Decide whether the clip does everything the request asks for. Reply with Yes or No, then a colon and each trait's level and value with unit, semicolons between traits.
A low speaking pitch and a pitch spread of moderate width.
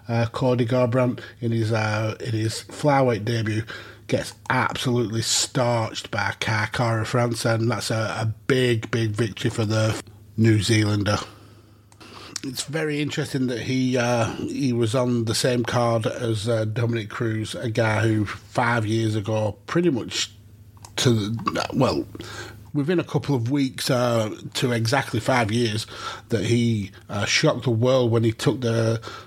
No: low, 115 Hz; narrow, 2.2 semitones